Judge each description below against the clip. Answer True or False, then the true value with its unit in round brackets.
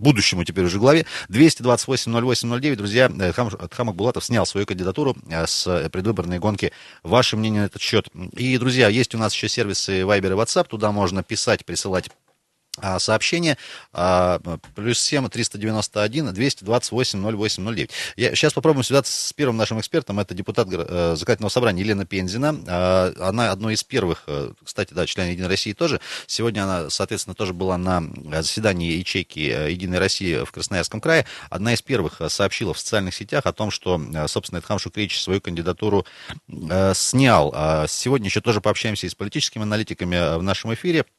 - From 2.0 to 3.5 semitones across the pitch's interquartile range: False (4.4 semitones)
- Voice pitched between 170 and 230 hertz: False (105 Hz)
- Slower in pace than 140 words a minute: False (150 wpm)